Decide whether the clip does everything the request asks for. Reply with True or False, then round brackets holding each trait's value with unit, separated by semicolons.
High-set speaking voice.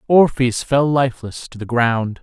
False (125 Hz)